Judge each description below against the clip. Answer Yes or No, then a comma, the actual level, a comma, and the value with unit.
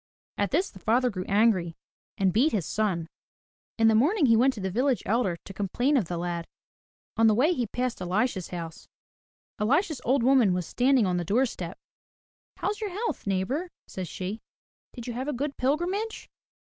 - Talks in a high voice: Yes, high, 225 Hz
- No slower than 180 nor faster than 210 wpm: Yes, average, 185 wpm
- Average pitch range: No, wide, 6.2 semitones